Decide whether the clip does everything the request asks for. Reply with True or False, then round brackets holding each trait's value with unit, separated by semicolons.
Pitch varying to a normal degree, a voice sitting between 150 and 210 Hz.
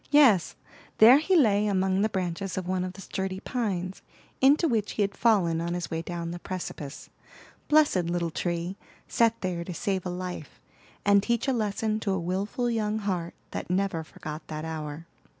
True (3.8 semitones; 190 Hz)